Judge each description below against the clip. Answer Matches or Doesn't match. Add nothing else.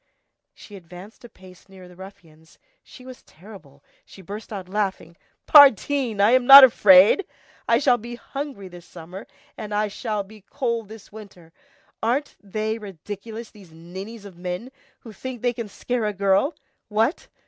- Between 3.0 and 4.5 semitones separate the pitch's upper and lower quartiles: Matches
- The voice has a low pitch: Doesn't match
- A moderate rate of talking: Matches